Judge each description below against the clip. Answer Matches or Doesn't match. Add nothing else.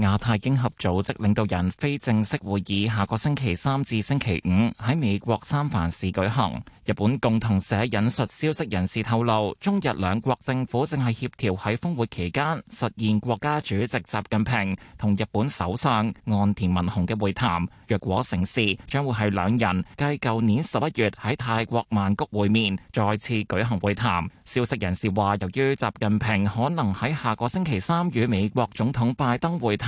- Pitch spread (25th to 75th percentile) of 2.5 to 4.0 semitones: Matches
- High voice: Doesn't match